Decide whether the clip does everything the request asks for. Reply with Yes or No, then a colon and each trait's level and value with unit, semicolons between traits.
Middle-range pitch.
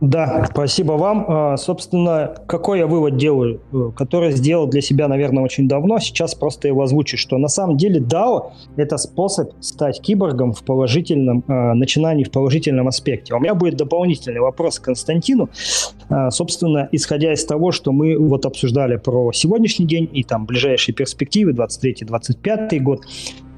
Yes: medium, 145 Hz